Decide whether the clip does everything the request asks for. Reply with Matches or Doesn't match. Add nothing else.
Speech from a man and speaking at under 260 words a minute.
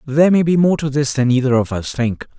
Doesn't match